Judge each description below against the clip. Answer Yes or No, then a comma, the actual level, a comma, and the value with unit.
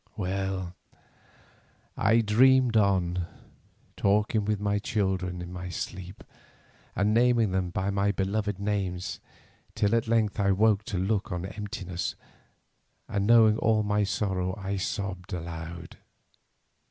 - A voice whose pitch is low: Yes, low, 100 Hz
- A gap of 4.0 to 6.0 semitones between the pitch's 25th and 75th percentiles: No, narrow, 2.4 semitones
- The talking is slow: Yes, slow, 125 wpm